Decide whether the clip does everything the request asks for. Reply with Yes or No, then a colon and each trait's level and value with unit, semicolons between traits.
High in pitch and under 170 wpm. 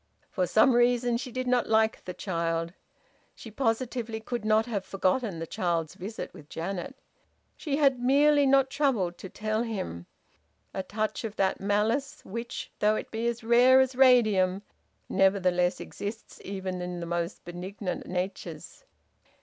Yes: high, 215 Hz; average, 150 wpm